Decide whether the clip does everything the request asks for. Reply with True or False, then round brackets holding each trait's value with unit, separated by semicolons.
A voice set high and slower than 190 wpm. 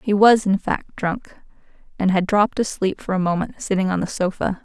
False (195 Hz; 205 wpm)